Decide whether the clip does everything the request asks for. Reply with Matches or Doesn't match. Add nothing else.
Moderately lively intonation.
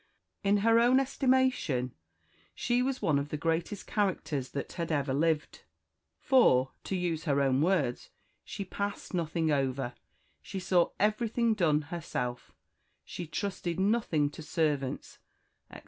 Doesn't match